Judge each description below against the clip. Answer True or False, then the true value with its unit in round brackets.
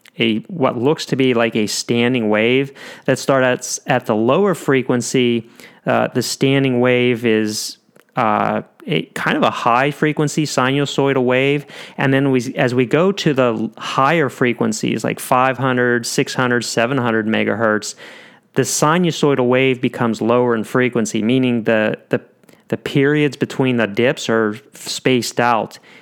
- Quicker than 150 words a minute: False (145 wpm)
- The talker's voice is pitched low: True (125 Hz)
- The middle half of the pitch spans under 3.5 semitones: True (2.8 semitones)